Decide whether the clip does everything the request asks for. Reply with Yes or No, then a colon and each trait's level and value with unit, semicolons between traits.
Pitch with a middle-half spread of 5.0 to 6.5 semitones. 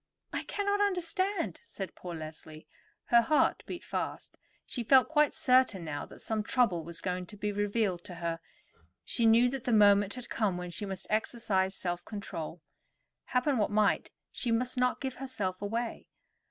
Yes: wide, 5.5 semitones